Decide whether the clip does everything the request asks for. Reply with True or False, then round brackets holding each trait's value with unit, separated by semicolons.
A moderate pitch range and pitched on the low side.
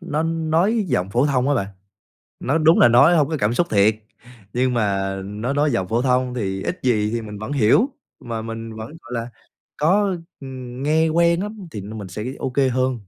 False (6.2 semitones; 125 Hz)